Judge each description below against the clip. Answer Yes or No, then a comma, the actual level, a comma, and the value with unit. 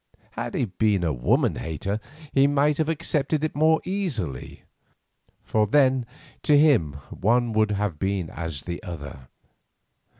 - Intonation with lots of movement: Yes, wide, 8.8 semitones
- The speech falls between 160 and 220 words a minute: No, average, 140 wpm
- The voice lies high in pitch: No, low, 110 Hz